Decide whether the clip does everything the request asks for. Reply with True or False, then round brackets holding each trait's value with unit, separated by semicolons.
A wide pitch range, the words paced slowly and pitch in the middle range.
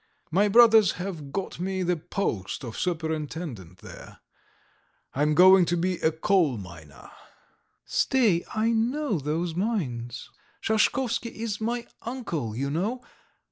True (6.8 semitones; 130 wpm; 180 Hz)